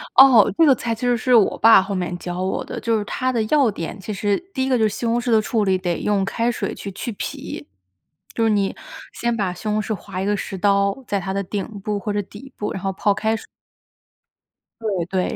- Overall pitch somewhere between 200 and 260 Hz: Yes, high, 210 Hz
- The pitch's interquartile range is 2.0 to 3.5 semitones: Yes, average, 2.9 semitones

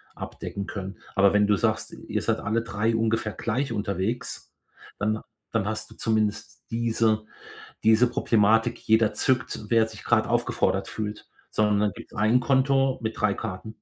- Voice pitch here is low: Yes, low, 110 Hz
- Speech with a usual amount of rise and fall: No, narrow, 1.6 semitones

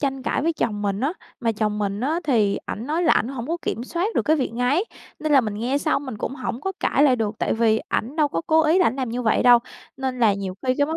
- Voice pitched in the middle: No, very high, 255 Hz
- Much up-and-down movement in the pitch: No, average, 5.0 semitones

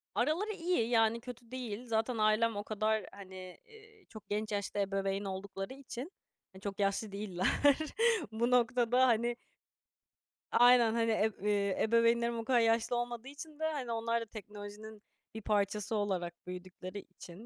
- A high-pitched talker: Yes, high, 220 Hz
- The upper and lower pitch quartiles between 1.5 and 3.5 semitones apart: Yes, average, 2.9 semitones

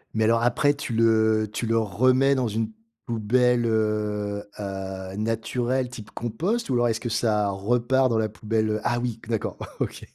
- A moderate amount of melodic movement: No, narrow, 2.3 semitones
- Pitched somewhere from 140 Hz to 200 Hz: No, low, 115 Hz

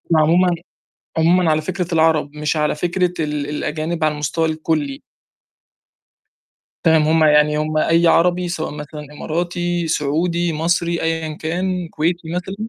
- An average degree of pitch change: No, narrow, 2.2 semitones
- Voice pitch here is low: No, medium, 160 Hz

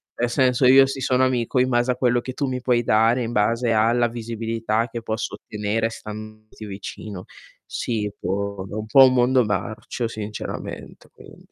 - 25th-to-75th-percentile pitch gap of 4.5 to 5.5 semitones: No, narrow, 2.5 semitones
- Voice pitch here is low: Yes, low, 115 Hz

